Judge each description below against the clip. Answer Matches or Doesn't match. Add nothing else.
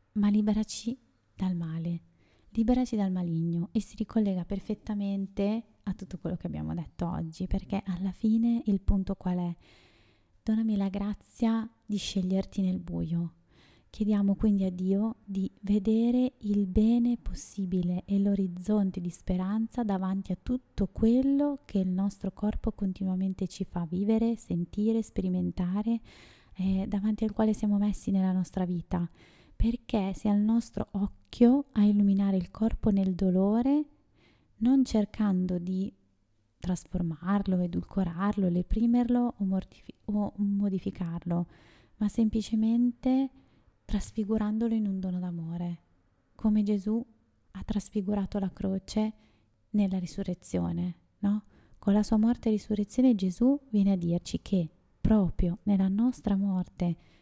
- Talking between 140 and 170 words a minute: Doesn't match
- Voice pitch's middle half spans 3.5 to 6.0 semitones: Doesn't match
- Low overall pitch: Doesn't match